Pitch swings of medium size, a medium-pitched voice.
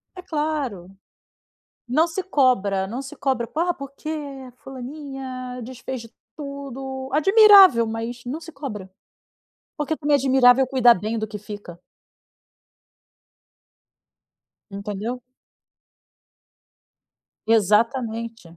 No: average, 3.9 semitones; very high, 255 Hz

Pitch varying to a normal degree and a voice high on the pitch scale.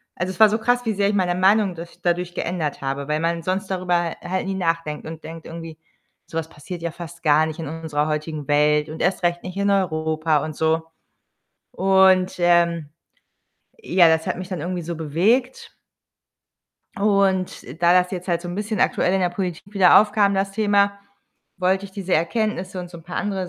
No: average, 3.0 semitones; medium, 175 Hz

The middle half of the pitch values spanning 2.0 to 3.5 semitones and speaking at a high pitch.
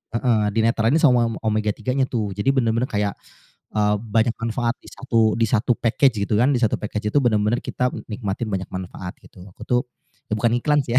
No: narrow, 2.6 semitones; low, 115 Hz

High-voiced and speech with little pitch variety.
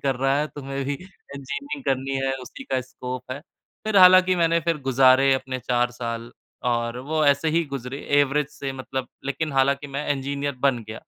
No: low, 135 Hz; narrow, 1.9 semitones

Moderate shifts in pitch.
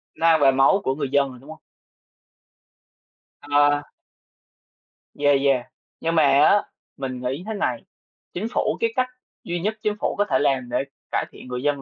Yes: average, 4.2 semitones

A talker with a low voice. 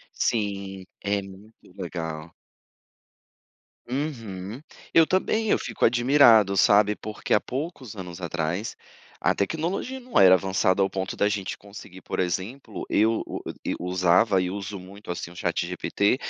Yes: low, 100 Hz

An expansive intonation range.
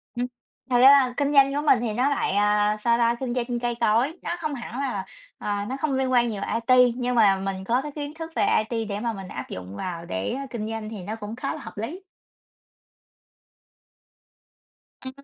No: average, 4.0 semitones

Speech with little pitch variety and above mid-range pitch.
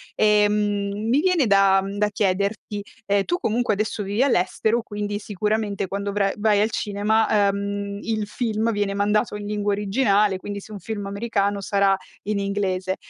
Yes: narrow, 1.2 semitones; high, 205 Hz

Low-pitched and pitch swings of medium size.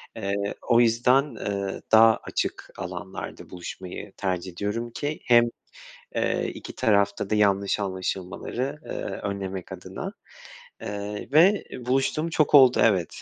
Yes: low, 105 Hz; average, 3.9 semitones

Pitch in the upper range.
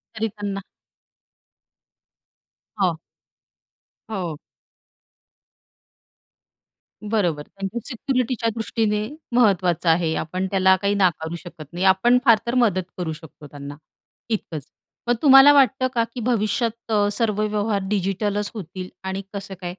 Yes: high, 200 Hz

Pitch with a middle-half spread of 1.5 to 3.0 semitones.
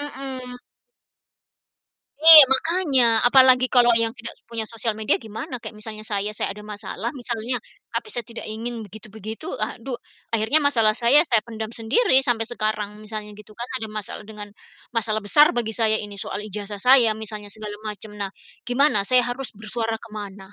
Yes: narrow, 2.6 semitones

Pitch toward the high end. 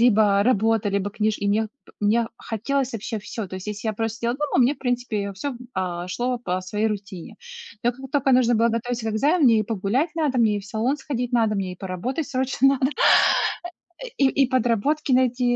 Yes: high, 230 Hz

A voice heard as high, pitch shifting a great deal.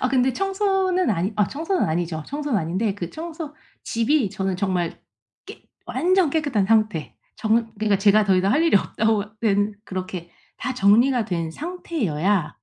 Yes: high, 215 Hz; wide, 7.5 semitones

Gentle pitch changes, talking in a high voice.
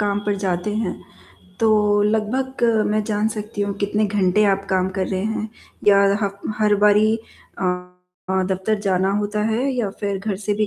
Yes: narrow, 1.9 semitones; high, 205 Hz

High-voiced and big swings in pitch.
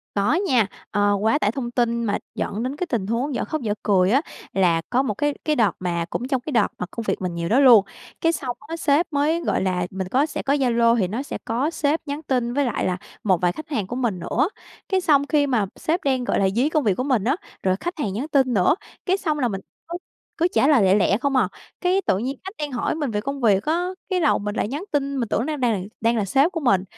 Yes: very high, 250 Hz; wide, 5.9 semitones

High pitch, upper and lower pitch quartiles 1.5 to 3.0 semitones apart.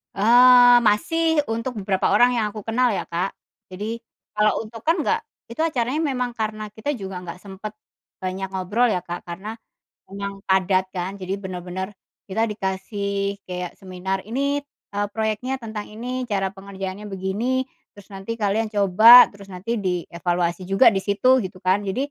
No: high, 205 Hz; average, 3.6 semitones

